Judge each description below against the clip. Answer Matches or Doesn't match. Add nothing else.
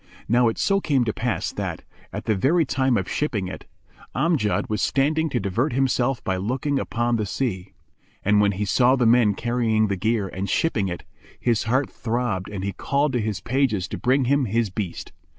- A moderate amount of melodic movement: Matches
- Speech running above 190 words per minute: Matches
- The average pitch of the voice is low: Matches